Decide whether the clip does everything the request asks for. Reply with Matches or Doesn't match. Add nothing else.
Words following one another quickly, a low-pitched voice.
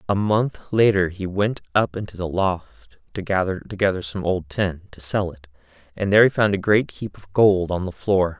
Matches